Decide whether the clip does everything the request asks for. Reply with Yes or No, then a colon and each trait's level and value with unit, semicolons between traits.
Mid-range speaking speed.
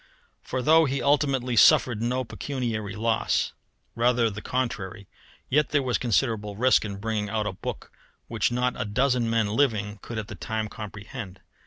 Yes: average, 165 wpm